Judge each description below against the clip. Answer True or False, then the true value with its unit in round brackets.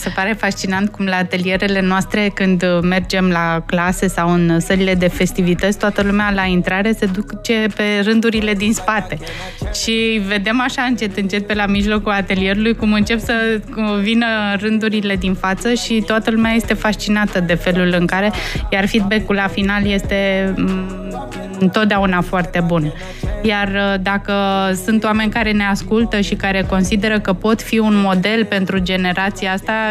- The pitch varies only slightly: True (2.3 semitones)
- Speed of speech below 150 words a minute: False (155 wpm)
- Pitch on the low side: False (200 Hz)